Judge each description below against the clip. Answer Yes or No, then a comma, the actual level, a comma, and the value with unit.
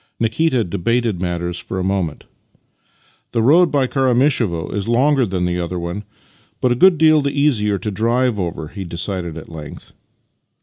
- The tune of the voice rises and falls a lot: Yes, wide, 6.5 semitones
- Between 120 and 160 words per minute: No, average, 170 wpm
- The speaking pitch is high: No, low, 105 Hz